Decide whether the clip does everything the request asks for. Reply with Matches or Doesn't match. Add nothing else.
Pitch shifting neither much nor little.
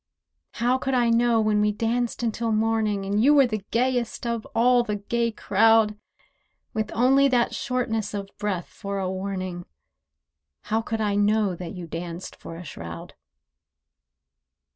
Matches